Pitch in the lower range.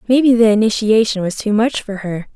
No: high, 215 Hz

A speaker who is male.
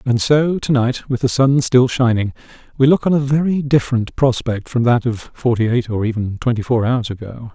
Yes: male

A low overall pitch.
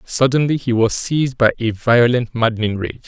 Yes: low, 120 Hz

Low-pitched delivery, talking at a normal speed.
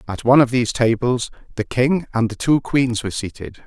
No: low, 120 Hz; fast, 215 wpm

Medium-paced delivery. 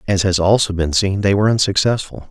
No: fast, 210 wpm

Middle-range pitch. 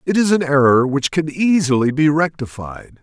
Yes: medium, 150 Hz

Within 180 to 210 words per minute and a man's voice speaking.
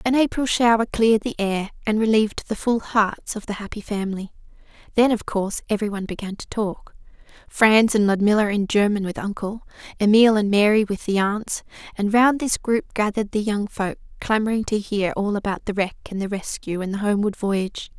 No: average, 185 wpm; female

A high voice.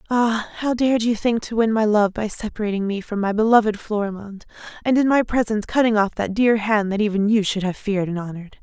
Yes: high, 215 Hz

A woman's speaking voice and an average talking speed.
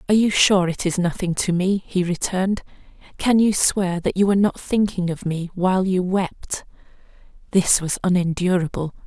Yes: female; average, 170 wpm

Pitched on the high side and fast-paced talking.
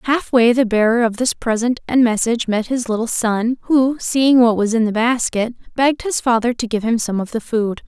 Yes: high, 235 Hz; fast, 220 wpm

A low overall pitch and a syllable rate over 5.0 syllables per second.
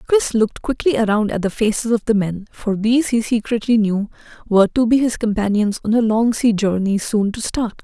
No: high, 220 Hz; 5.5 syllables/s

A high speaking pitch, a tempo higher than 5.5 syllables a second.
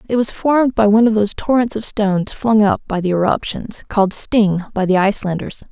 Yes: high, 210 Hz; 5.8 syllables/s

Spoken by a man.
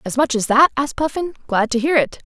No: female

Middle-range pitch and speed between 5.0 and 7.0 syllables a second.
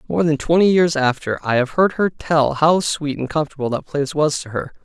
Yes: medium, 150 Hz; 5.5 syllables/s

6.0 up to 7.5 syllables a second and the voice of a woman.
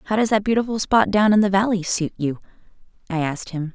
Yes: 6.4 syllables/s; female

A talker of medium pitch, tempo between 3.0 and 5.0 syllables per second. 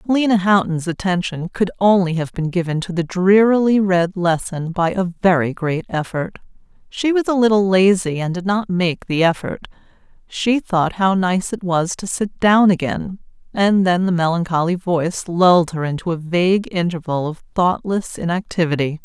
Yes: medium, 180 Hz; 4.8 syllables/s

